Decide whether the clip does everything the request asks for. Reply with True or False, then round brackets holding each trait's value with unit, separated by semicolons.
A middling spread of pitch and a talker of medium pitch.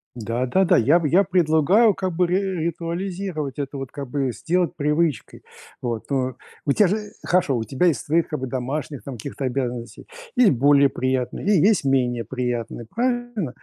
False (5.8 semitones; 145 Hz)